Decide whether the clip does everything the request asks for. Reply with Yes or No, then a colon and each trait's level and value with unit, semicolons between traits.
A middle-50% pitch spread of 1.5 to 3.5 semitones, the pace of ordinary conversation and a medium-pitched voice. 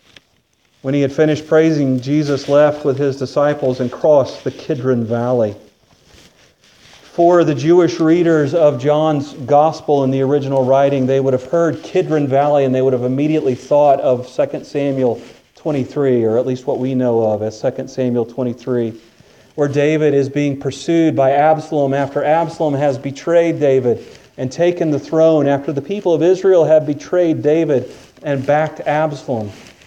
Yes: average, 2.9 semitones; average, 160 wpm; medium, 145 Hz